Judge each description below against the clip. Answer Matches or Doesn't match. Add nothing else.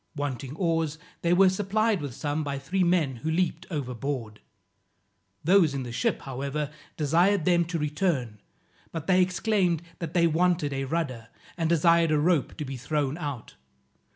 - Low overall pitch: Doesn't match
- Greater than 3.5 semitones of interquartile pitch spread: Matches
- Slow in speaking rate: Doesn't match